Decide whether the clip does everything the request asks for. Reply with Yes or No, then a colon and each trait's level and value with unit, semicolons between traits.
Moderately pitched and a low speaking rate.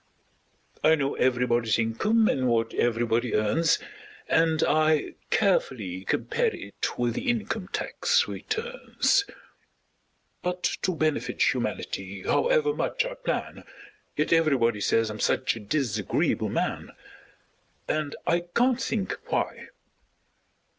Yes: medium, 150 Hz; slow, 115 wpm